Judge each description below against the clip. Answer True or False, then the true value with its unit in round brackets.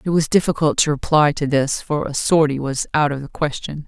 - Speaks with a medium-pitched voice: True (150 Hz)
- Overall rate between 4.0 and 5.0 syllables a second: False (5.4 syllables/s)